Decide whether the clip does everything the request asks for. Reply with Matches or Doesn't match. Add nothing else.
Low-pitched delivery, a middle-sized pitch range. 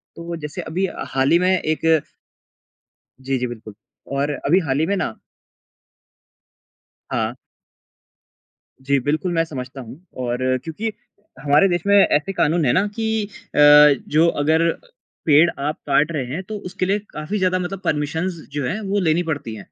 Doesn't match